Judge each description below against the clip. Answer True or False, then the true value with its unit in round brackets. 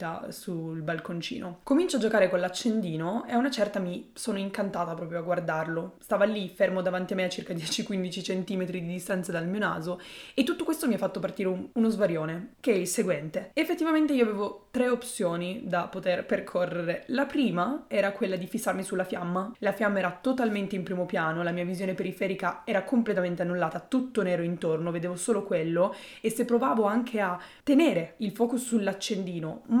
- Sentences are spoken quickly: True (185 wpm)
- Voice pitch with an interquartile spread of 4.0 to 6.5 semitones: True (4.3 semitones)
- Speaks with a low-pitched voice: False (195 Hz)